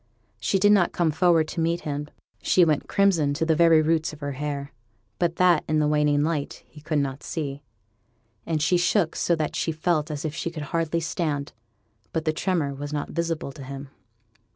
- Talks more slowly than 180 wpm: No, average, 200 wpm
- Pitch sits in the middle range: Yes, medium, 155 Hz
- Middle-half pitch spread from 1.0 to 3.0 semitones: Yes, narrow, 2.4 semitones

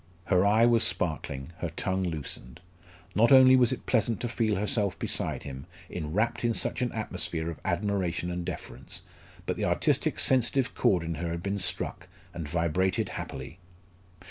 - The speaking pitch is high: No, very low, 95 Hz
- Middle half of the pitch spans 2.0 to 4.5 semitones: No, average, 5.2 semitones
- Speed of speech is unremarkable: Yes, average, 165 wpm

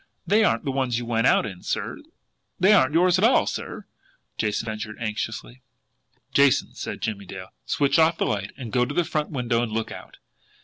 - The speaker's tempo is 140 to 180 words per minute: No, average, 195 wpm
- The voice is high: No, low, 120 Hz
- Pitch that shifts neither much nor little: No, wide, 5.7 semitones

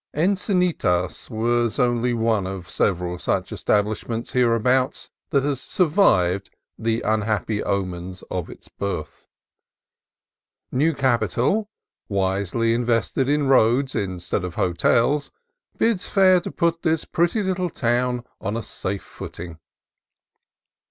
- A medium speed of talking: No, slow, 120 wpm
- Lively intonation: Yes, wide, 6.4 semitones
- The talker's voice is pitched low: Yes, low, 115 Hz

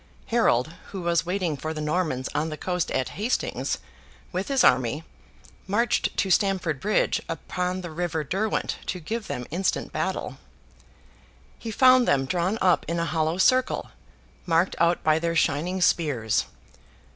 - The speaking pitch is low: No, medium, 175 Hz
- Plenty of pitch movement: No, average, 3.6 semitones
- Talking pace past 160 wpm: No, average, 150 wpm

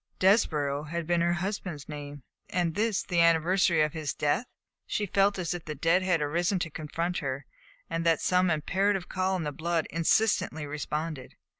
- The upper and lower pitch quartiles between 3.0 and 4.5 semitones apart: Yes, average, 3.3 semitones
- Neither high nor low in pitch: Yes, medium, 170 Hz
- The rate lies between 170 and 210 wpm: Yes, average, 175 wpm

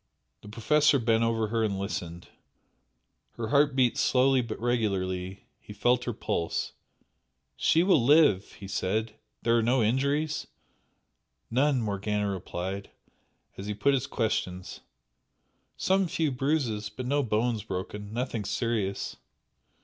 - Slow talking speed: Yes, slow, 130 wpm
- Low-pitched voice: Yes, low, 115 Hz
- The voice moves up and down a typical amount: Yes, average, 4.4 semitones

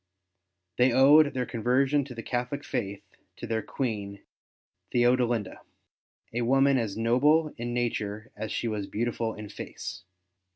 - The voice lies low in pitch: Yes, low, 120 Hz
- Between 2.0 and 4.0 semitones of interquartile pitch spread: Yes, average, 3.0 semitones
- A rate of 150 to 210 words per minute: No, slow, 135 wpm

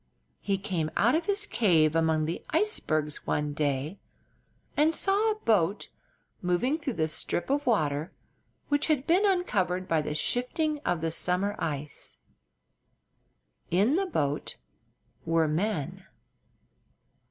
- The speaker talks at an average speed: No, slow, 130 wpm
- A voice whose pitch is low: No, medium, 185 Hz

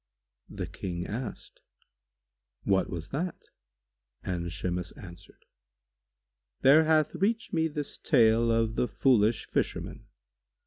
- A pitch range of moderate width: No, wide, 8.4 semitones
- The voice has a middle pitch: No, low, 115 Hz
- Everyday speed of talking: No, slow, 105 wpm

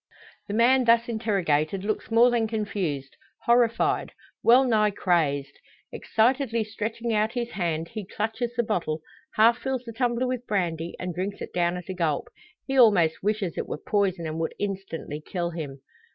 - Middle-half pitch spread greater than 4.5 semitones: Yes, average, 5.2 semitones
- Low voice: No, high, 210 Hz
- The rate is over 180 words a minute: No, average, 165 wpm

